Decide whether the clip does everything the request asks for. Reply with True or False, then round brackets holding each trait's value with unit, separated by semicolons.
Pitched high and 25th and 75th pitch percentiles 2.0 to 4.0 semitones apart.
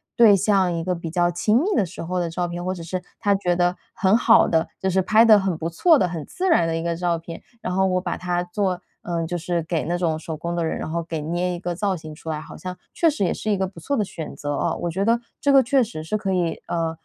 False (175 Hz; 2.8 semitones)